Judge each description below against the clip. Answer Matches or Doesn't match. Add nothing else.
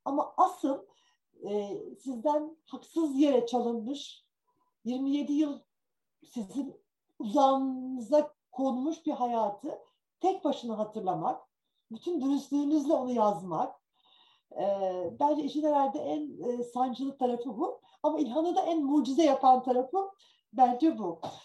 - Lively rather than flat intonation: Doesn't match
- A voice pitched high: Matches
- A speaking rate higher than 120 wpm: Doesn't match